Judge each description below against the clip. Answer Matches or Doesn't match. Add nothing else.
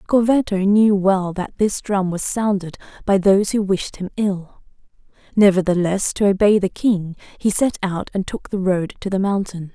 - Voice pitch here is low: Doesn't match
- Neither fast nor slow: Matches